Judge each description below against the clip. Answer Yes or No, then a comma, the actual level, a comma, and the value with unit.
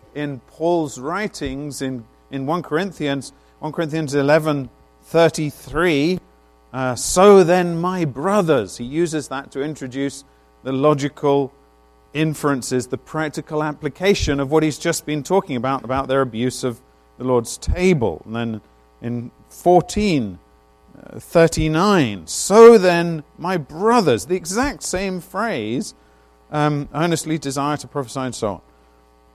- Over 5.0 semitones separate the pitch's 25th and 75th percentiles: Yes, wide, 5.4 semitones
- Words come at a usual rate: No, slow, 125 wpm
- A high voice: No, medium, 145 Hz